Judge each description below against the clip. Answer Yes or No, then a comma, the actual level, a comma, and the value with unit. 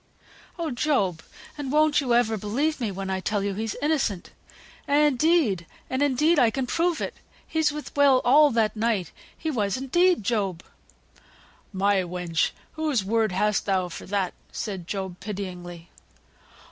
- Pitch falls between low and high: No, high, 225 Hz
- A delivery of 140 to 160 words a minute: Yes, average, 155 wpm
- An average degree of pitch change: No, wide, 7.1 semitones